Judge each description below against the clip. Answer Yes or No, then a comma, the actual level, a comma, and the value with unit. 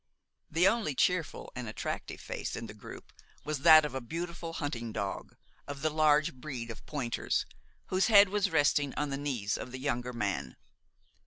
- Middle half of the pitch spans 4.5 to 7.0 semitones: Yes, average, 4.9 semitones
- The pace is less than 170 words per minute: No, average, 175 wpm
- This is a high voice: No, medium, 145 Hz